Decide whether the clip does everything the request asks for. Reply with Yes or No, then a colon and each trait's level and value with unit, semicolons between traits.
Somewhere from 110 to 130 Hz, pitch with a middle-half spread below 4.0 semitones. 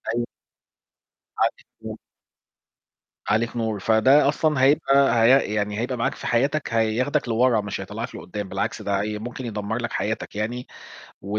Yes: low, 115 Hz; average, 3.3 semitones